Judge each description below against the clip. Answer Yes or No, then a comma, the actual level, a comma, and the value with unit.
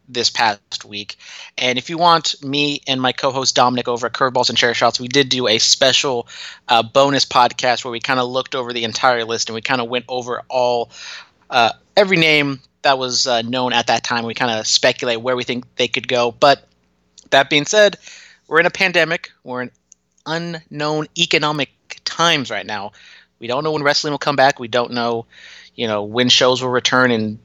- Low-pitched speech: Yes, low, 125 Hz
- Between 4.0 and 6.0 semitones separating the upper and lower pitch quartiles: No, average, 3.0 semitones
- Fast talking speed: Yes, fast, 210 wpm